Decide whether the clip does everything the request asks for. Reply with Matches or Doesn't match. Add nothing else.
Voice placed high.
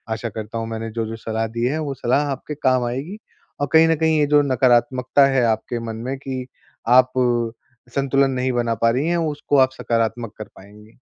Doesn't match